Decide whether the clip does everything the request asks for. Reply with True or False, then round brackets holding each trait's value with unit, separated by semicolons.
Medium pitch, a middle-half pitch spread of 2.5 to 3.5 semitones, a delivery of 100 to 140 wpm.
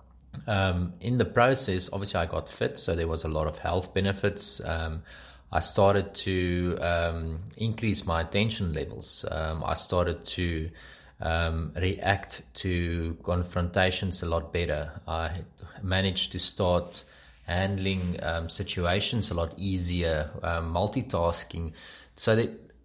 False (90 Hz; 2.8 semitones; 135 wpm)